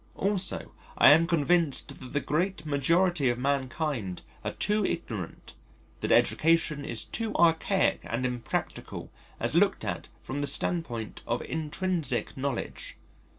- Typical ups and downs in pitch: Yes, average, 4.8 semitones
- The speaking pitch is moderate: Yes, medium, 150 Hz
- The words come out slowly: Yes, slow, 130 wpm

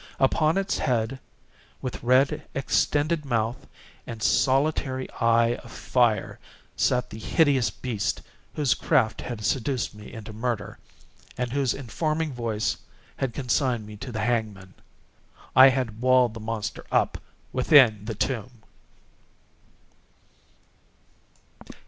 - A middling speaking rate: No, slow, 115 wpm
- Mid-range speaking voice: No, low, 125 Hz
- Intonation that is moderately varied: Yes, average, 3.1 semitones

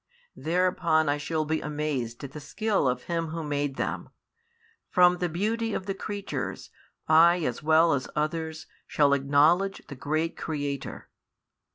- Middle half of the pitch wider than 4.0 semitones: No, average, 3.3 semitones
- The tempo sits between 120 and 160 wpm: Yes, average, 150 wpm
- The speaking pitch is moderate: Yes, medium, 155 Hz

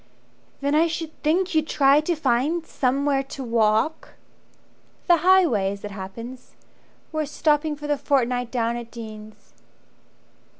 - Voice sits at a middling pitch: No, very high, 275 Hz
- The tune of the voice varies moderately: Yes, average, 5.0 semitones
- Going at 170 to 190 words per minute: No, average, 140 wpm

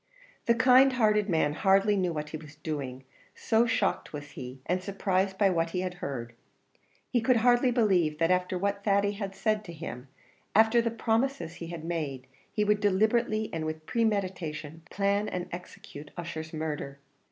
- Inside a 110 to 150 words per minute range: No, average, 175 wpm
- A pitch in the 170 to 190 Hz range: Yes, medium, 185 Hz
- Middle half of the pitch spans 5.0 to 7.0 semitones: Yes, average, 5.3 semitones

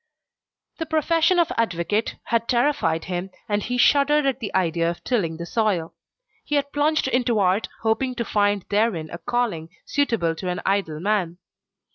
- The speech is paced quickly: No, average, 165 wpm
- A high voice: Yes, high, 215 Hz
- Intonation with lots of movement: Yes, wide, 6.9 semitones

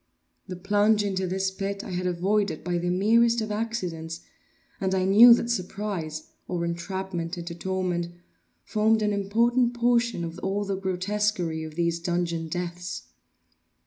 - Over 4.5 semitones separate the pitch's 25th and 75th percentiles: No, average, 3.3 semitones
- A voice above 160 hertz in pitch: Yes, high, 190 Hz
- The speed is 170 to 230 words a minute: No, average, 145 wpm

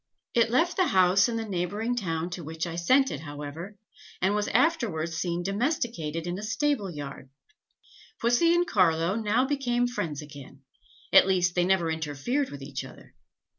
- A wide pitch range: Yes, wide, 6.7 semitones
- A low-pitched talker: No, high, 190 Hz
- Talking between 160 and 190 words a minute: Yes, average, 170 wpm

